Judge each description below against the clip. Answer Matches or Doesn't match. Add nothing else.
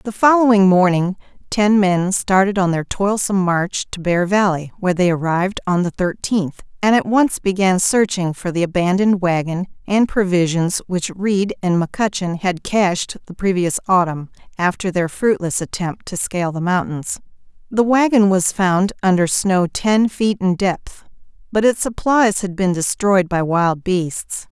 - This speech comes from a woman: Matches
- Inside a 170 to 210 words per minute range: Doesn't match